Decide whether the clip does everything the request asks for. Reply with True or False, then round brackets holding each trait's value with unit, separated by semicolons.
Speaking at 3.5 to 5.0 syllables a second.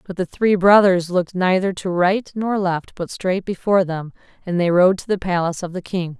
False (5.3 syllables/s)